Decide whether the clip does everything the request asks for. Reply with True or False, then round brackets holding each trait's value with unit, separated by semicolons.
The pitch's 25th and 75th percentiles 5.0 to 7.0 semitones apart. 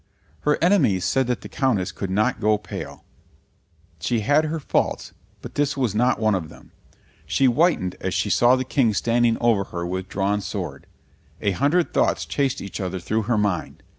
True (5.3 semitones)